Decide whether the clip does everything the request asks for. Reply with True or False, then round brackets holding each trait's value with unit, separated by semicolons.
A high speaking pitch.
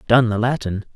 False (115 Hz)